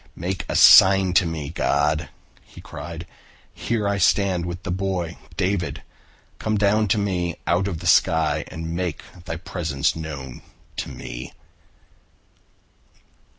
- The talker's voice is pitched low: Yes, very low, 85 Hz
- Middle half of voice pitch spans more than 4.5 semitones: No, average, 3.2 semitones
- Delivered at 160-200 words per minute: No, slow, 135 wpm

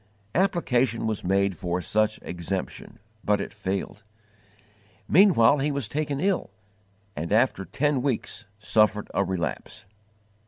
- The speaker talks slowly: Yes, slow, 120 wpm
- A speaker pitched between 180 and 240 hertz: No, low, 110 Hz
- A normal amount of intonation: No, wide, 6.4 semitones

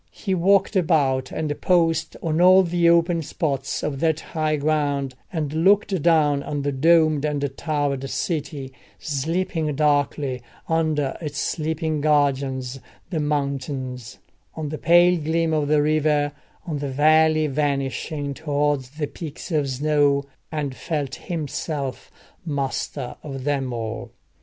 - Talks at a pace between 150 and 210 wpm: No, slow, 135 wpm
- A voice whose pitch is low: No, medium, 150 Hz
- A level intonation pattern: Yes, narrow, 2.3 semitones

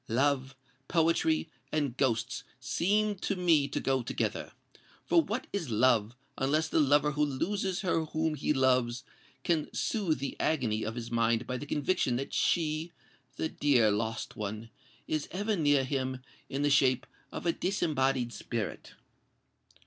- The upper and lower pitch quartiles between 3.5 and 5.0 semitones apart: Yes, average, 4.3 semitones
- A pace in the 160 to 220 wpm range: No, average, 145 wpm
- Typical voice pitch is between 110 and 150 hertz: Yes, medium, 140 Hz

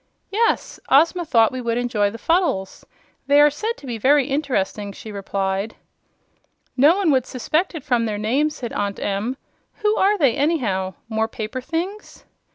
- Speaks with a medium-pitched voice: No, very high, 255 Hz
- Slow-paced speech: No, average, 165 wpm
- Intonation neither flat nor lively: No, wide, 6.2 semitones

